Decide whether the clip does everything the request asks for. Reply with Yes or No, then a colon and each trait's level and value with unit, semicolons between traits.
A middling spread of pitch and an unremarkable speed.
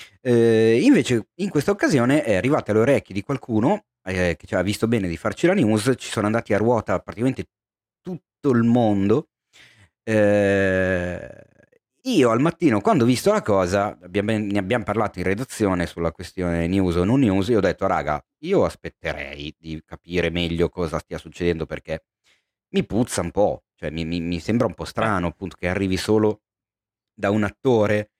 No: average, 4.0 semitones; fast, 175 wpm